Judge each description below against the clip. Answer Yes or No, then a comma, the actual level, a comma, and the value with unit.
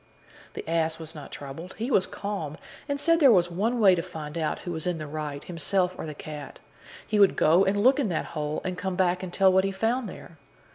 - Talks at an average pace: No, fast, 240 wpm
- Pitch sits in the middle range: Yes, medium, 180 Hz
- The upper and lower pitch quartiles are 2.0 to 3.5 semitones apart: No, average, 4.0 semitones